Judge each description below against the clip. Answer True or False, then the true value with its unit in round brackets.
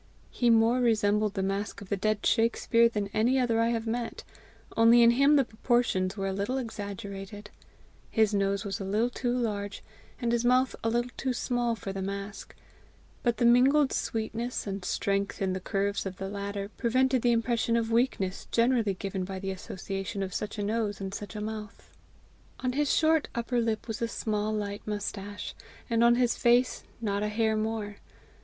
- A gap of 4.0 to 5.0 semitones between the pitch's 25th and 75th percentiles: False (2.9 semitones)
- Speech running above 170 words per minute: True (190 wpm)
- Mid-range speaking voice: False (220 Hz)